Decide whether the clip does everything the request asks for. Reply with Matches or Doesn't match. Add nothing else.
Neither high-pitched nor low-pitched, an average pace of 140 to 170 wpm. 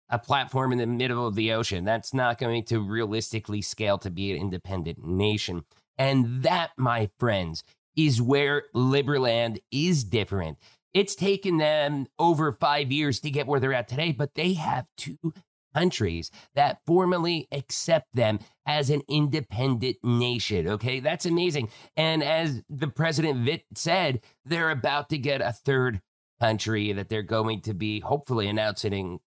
Doesn't match